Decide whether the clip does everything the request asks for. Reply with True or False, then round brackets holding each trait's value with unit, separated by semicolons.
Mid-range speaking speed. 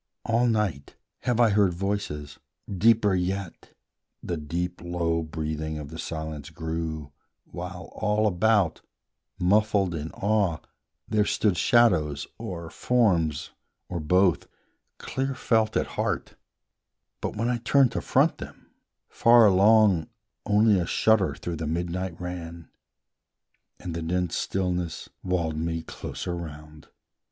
False (125 wpm)